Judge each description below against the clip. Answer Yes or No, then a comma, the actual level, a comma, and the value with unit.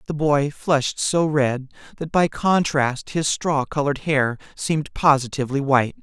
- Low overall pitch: No, medium, 145 Hz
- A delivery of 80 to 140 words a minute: No, average, 150 wpm